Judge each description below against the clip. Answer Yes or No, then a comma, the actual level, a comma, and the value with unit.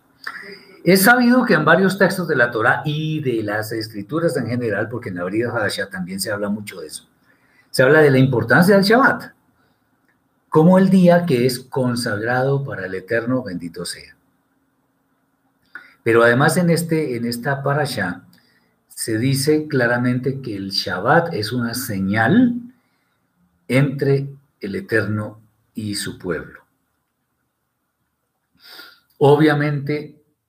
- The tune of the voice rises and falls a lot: Yes, wide, 5.7 semitones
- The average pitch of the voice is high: No, low, 135 Hz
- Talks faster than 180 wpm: No, average, 130 wpm